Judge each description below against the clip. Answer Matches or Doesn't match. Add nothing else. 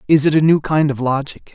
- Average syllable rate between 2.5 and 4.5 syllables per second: Doesn't match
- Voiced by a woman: Doesn't match